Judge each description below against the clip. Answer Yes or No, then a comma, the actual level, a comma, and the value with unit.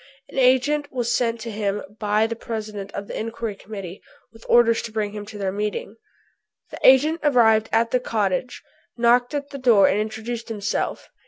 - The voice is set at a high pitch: Yes, high, 225 Hz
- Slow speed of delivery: No, average, 180 wpm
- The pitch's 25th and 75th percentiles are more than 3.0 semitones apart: No, average, 2.7 semitones